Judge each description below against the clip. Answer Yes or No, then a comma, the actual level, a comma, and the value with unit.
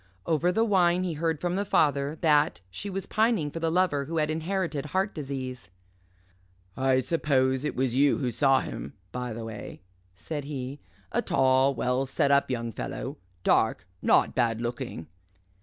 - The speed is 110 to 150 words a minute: No, average, 170 wpm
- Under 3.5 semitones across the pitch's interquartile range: No, average, 4.2 semitones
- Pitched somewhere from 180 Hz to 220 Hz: No, medium, 140 Hz